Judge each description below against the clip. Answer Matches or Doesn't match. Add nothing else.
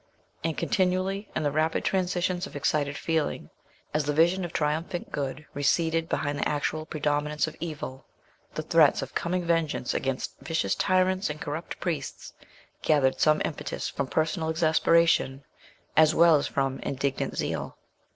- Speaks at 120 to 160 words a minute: Matches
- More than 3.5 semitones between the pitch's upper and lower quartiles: Doesn't match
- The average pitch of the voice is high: Doesn't match